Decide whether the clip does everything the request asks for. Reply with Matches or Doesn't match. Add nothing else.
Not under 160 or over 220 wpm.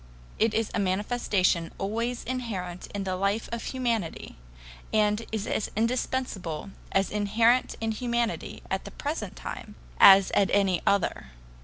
Doesn't match